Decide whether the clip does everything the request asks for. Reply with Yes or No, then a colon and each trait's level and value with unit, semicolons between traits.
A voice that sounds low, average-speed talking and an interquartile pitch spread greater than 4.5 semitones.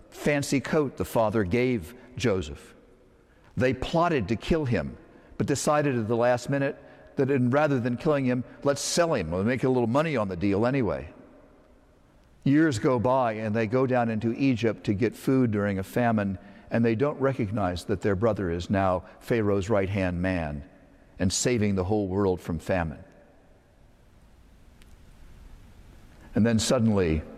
Yes: low, 115 Hz; average, 160 wpm; average, 5.0 semitones